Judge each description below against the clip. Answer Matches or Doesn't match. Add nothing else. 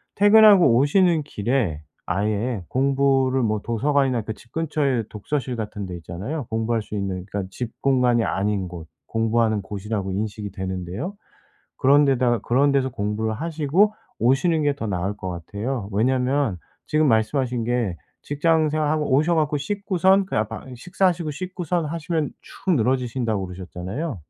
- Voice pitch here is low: Matches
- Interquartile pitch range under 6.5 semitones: Matches